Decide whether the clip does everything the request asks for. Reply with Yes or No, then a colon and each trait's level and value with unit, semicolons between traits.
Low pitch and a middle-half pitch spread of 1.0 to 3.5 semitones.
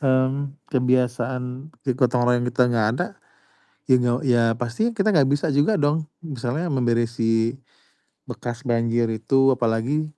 Yes: low, 125 Hz; average, 3.0 semitones